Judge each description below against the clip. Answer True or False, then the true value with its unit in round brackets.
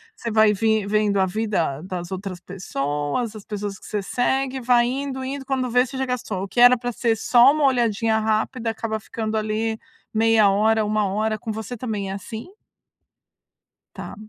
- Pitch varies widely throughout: False (3.2 semitones)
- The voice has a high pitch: True (220 Hz)